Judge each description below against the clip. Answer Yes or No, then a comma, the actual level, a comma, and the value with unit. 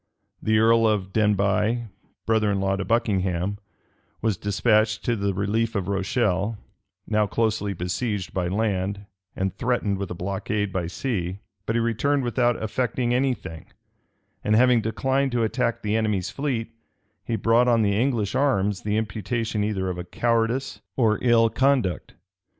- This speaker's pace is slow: No, average, 150 wpm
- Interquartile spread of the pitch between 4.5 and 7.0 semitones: No, average, 3.0 semitones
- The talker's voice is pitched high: No, low, 110 Hz